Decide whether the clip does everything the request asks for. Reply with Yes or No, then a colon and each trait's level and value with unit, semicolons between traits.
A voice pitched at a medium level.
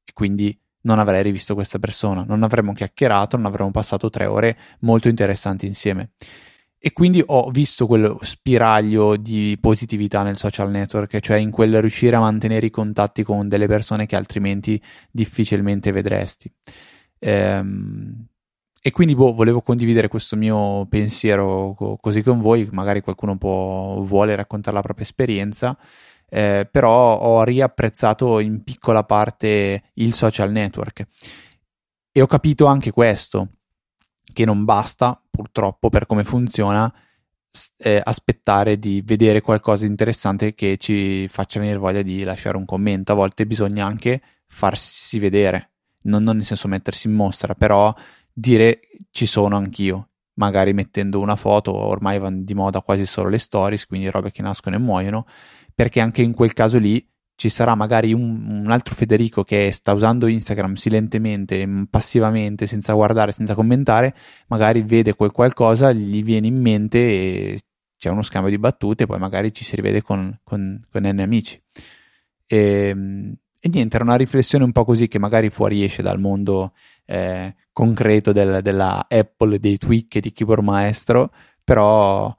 No: low, 105 Hz